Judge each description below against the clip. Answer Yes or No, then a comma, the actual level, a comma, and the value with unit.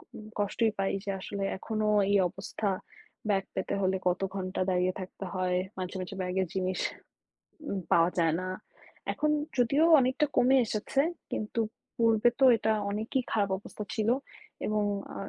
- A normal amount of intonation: Yes, average, 3.2 semitones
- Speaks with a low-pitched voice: No, high, 205 Hz